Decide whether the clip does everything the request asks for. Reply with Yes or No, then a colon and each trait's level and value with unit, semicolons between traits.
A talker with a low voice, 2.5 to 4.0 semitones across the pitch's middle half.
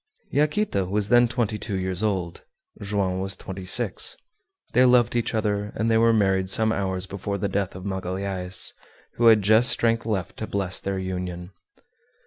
Yes: low, 100 Hz; average, 2.9 semitones